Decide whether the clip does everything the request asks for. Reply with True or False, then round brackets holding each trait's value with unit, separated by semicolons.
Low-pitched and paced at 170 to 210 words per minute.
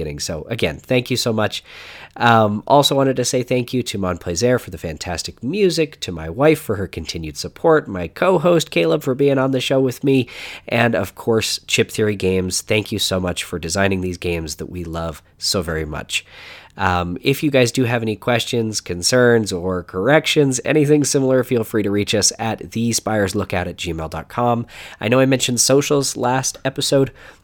True (110 Hz; 190 wpm)